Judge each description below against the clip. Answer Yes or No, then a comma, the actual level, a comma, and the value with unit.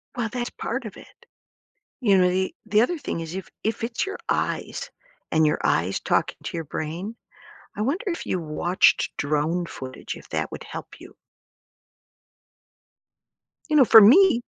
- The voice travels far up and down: Yes, wide, 6.7 semitones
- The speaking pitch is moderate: No, high, 200 Hz